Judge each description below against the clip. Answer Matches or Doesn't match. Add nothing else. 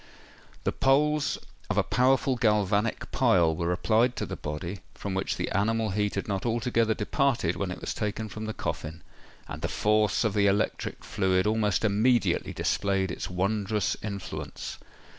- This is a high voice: Doesn't match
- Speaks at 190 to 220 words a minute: Doesn't match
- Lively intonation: Doesn't match